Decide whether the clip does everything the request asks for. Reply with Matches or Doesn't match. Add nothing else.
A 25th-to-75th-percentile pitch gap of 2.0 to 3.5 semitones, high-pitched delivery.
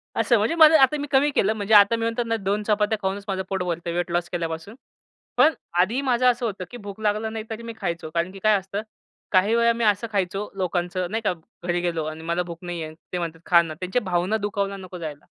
Doesn't match